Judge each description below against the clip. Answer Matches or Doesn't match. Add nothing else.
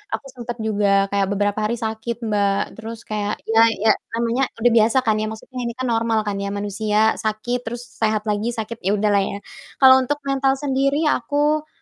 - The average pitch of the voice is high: Matches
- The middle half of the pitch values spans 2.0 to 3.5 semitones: Matches